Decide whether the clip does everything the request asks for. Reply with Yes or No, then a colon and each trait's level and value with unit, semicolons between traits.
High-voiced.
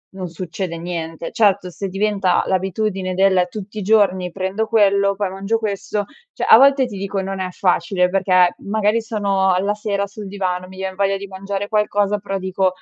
Yes: high, 195 Hz